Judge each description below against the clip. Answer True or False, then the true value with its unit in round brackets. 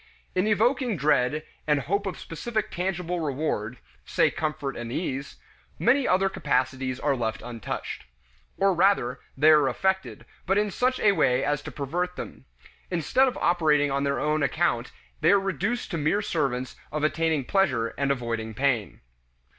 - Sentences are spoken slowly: False (160 wpm)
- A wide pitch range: True (6.2 semitones)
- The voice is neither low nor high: True (155 Hz)